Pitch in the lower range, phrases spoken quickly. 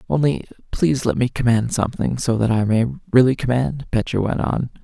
No: low, 120 Hz; average, 185 wpm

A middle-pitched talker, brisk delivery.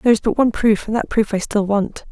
No: high, 215 Hz; fast, 315 wpm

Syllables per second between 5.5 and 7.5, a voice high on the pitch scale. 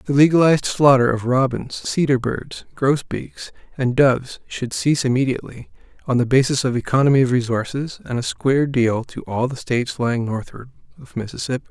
No: 5.6 syllables/s; low, 130 Hz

